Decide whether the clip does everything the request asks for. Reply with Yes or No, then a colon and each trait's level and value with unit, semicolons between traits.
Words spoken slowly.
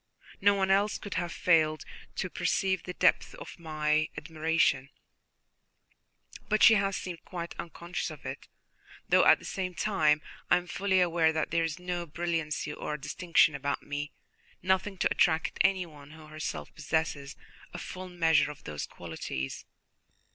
No: average, 155 wpm